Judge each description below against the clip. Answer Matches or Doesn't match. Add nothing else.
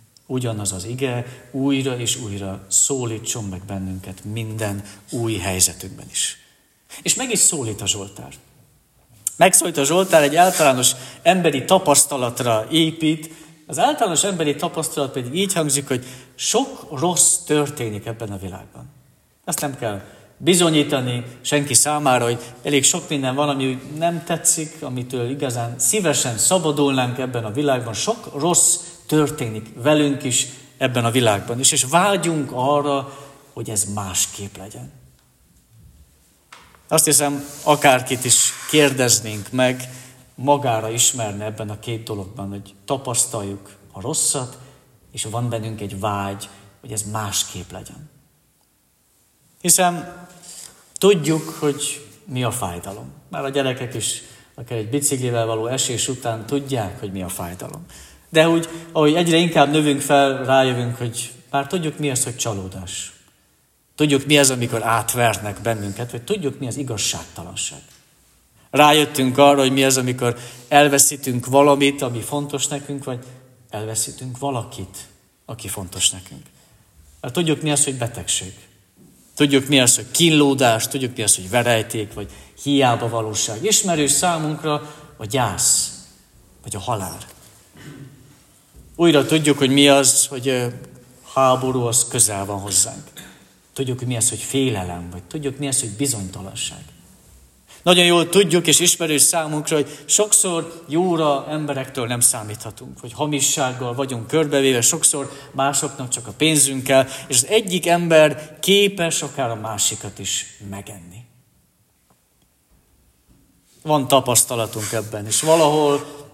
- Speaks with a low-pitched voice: Matches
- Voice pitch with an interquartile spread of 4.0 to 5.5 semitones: Matches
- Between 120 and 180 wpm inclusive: Matches